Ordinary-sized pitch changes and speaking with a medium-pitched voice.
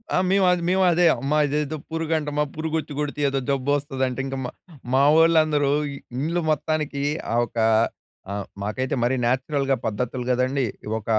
Yes: average, 3.2 semitones; medium, 145 Hz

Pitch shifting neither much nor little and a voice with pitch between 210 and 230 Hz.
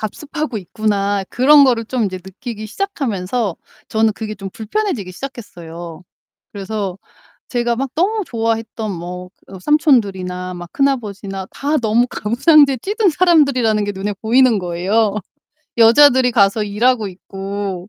Yes: average, 4.8 semitones; high, 220 Hz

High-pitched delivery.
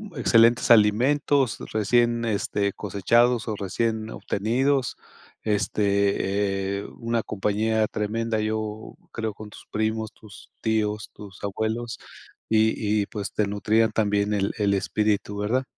No: low, 110 Hz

